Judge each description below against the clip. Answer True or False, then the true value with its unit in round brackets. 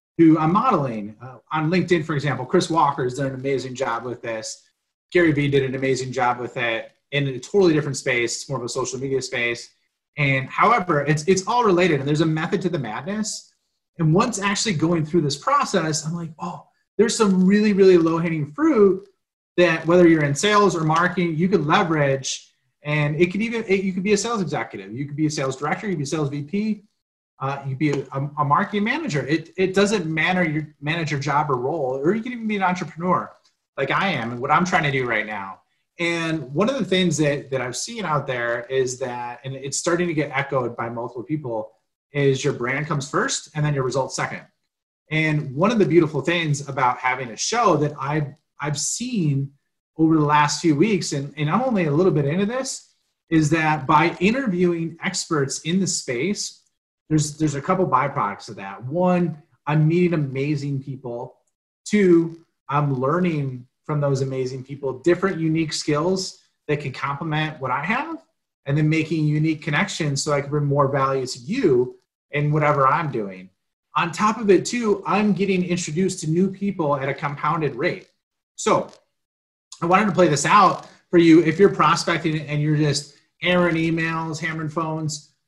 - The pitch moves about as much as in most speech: True (4.5 semitones)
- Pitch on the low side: False (155 Hz)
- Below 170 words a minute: False (200 wpm)